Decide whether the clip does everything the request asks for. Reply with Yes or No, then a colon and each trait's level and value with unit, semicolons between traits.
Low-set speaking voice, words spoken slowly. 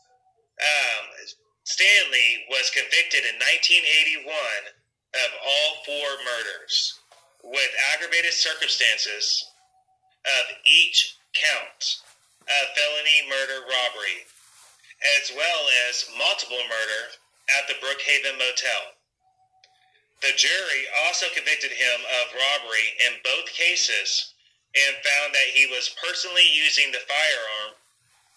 No: medium, 150 Hz; slow, 100 wpm